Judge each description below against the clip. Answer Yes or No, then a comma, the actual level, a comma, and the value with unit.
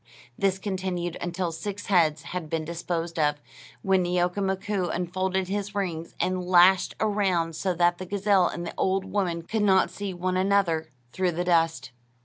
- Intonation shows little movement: Yes, narrow, 2.1 semitones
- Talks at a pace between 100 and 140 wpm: No, average, 165 wpm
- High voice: No, medium, 180 Hz